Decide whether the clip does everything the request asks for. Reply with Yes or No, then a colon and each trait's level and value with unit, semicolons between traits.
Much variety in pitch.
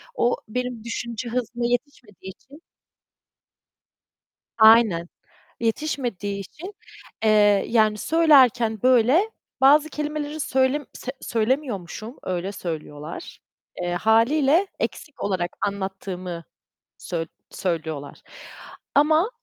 Yes: wide, 6.1 semitones